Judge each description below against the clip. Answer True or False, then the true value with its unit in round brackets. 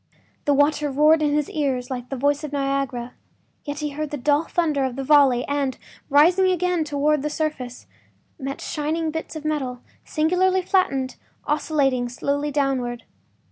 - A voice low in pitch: False (290 Hz)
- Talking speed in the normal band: True (160 wpm)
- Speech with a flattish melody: True (2.3 semitones)